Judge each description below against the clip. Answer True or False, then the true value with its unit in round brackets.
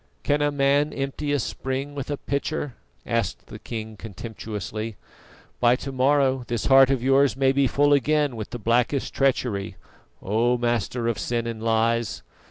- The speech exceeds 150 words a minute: True (165 wpm)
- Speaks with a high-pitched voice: False (125 Hz)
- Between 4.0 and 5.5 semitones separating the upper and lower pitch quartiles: False (3.3 semitones)